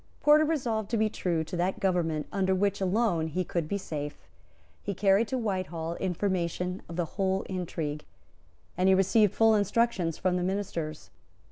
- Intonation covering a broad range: No, average, 3.2 semitones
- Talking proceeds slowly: No, average, 165 wpm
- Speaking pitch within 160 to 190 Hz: Yes, medium, 185 Hz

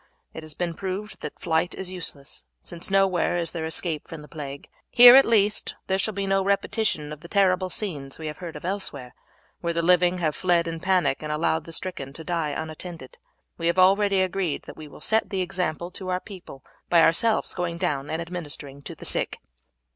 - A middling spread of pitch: Yes, average, 3.3 semitones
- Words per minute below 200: No, fast, 205 wpm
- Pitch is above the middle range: No, medium, 175 Hz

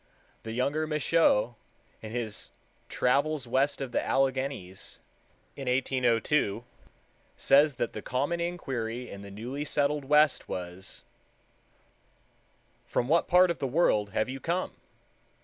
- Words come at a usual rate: No, slow, 125 wpm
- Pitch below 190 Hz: Yes, low, 135 Hz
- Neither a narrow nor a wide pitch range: Yes, average, 4.5 semitones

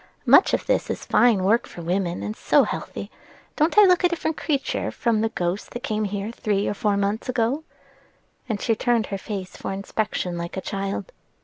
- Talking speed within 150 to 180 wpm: No, average, 200 wpm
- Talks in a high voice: Yes, high, 215 Hz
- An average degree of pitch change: Yes, average, 3.6 semitones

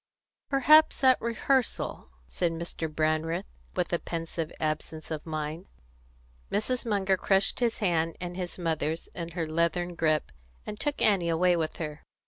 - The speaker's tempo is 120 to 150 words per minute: Yes, average, 145 wpm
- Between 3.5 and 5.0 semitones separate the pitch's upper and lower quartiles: Yes, average, 3.9 semitones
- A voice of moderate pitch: Yes, medium, 170 Hz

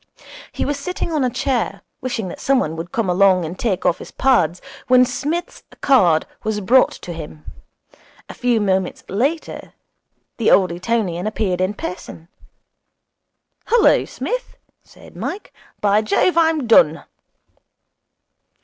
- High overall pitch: Yes, high, 215 Hz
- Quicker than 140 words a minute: No, slow, 135 wpm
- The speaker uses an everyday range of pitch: No, wide, 6.4 semitones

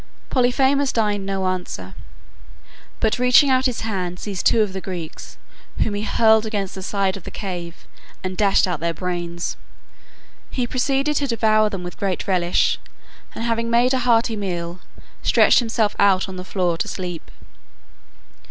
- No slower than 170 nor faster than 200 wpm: No, average, 160 wpm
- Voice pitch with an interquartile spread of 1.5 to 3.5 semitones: No, average, 4.2 semitones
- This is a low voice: No, high, 200 Hz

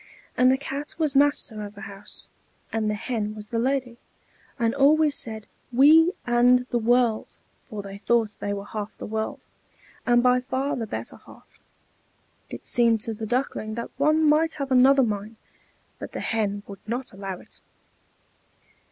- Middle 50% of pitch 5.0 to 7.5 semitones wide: No, average, 3.9 semitones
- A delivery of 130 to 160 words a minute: No, average, 170 wpm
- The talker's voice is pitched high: Yes, high, 235 Hz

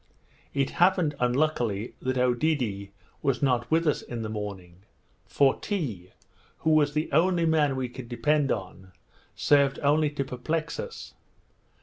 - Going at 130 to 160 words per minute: Yes, average, 140 wpm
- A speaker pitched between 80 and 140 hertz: Yes, low, 135 Hz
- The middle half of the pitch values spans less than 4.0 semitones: No, average, 4.5 semitones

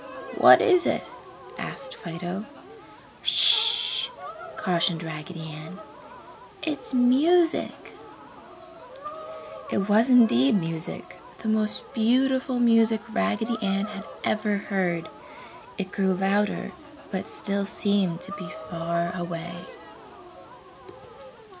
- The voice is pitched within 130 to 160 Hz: No, high, 200 Hz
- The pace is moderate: No, slow, 95 wpm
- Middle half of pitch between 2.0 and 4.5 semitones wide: No, average, 5.3 semitones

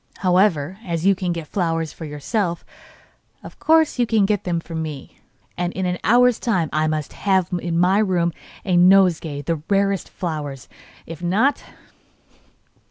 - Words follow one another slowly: No, average, 165 wpm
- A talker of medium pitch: Yes, medium, 175 Hz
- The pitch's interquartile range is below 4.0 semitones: Yes, average, 3.3 semitones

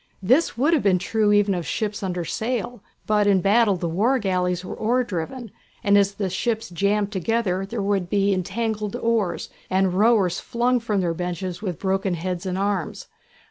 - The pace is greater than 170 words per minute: Yes, average, 180 wpm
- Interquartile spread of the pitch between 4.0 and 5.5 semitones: No, average, 3.3 semitones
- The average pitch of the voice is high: Yes, high, 200 Hz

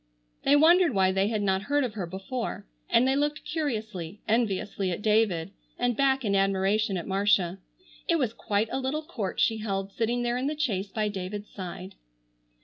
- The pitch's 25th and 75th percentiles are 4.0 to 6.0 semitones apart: Yes, average, 4.7 semitones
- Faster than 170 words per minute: Yes, average, 185 wpm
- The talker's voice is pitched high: Yes, high, 215 Hz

